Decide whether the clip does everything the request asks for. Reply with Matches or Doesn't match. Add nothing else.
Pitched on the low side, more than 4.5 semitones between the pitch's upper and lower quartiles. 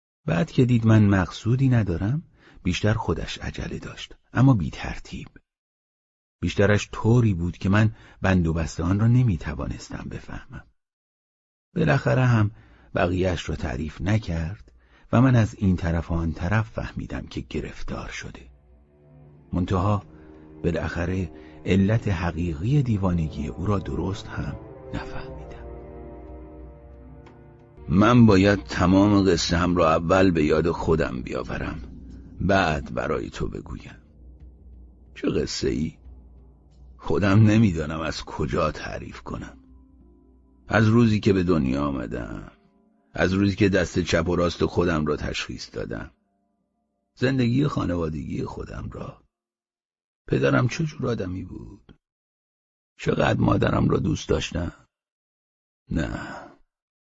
Matches